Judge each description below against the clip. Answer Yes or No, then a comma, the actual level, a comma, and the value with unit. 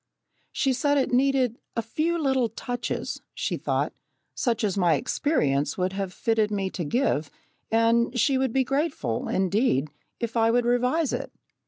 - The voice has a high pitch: Yes, high, 235 Hz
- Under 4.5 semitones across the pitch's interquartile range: No, average, 5.2 semitones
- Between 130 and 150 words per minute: No, average, 160 wpm